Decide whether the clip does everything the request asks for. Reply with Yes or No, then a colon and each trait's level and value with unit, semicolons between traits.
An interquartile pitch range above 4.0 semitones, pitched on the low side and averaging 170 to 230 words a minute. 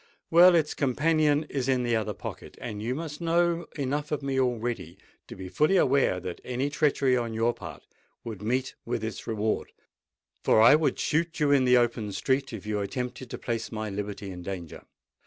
Yes: average, 5.2 semitones; low, 125 Hz; average, 195 wpm